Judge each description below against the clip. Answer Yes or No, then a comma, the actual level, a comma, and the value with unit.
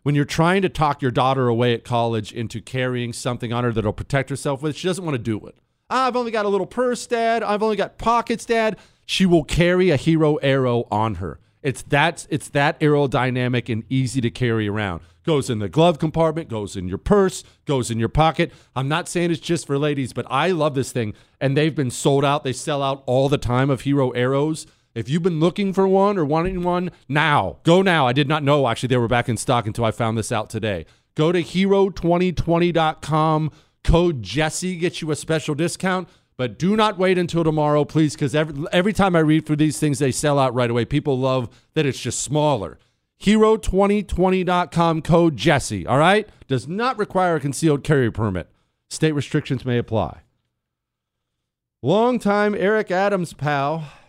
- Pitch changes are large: Yes, wide, 5.8 semitones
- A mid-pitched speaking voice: Yes, medium, 150 Hz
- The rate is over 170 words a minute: Yes, average, 200 wpm